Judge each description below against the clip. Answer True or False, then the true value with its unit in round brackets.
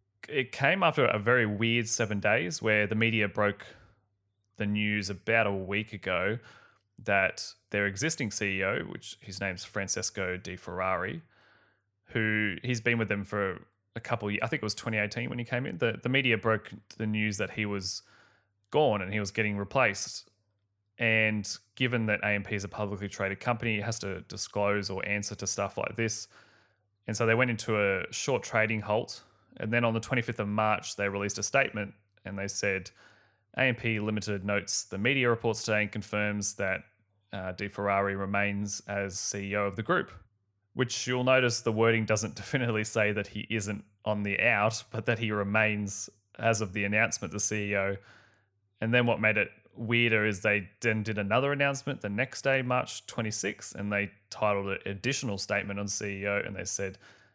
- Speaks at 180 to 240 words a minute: True (185 wpm)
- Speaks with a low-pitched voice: True (105 Hz)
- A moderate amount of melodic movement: False (2.0 semitones)